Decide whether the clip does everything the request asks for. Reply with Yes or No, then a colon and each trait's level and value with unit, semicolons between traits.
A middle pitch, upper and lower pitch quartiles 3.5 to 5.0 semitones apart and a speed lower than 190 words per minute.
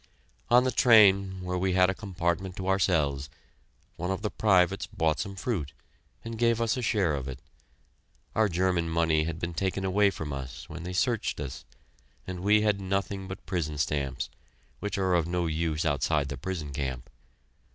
No: very low, 90 Hz; average, 4.0 semitones; average, 180 wpm